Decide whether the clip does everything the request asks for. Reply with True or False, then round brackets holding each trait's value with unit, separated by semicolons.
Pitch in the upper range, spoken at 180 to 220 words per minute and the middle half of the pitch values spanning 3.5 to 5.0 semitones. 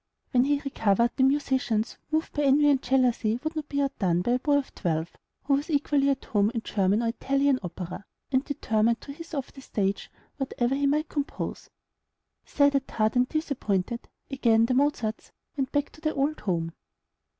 True (265 Hz; 185 wpm; 4.3 semitones)